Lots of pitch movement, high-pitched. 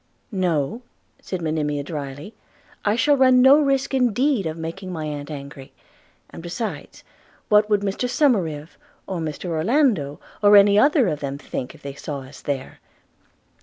No: wide, 7.5 semitones; medium, 175 Hz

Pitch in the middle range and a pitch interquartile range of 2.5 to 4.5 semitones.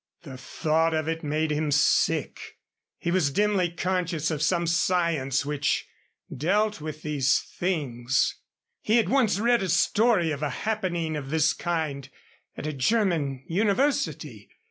Yes: medium, 160 Hz; average, 4.1 semitones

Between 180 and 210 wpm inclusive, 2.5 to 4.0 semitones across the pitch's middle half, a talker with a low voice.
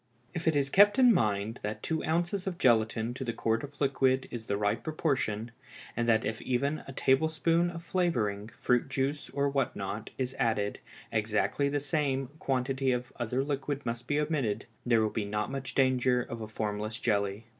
No: average, 190 wpm; average, 4.6 semitones; low, 130 Hz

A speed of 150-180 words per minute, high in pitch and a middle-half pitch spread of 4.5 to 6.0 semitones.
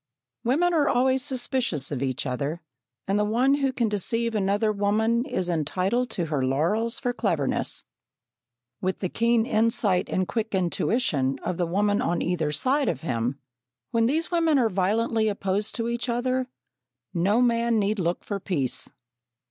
Yes: average, 160 wpm; high, 210 Hz; wide, 5.4 semitones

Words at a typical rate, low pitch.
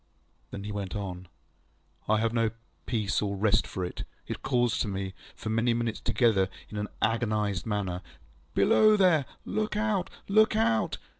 Yes: average, 165 wpm; low, 110 Hz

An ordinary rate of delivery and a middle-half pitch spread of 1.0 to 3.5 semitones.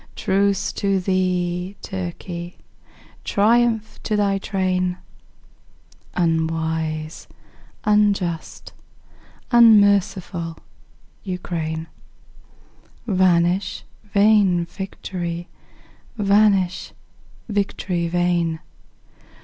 No: slow, 55 wpm; average, 2.8 semitones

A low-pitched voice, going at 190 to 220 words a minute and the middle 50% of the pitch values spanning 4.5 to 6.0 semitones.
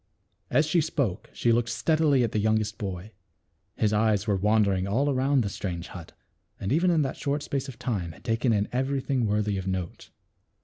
Yes: low, 110 Hz; average, 195 wpm; average, 5.2 semitones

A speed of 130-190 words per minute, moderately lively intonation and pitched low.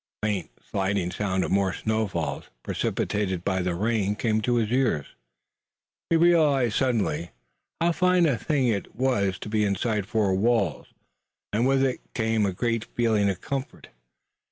Yes: average, 160 wpm; average, 4.2 semitones; low, 110 Hz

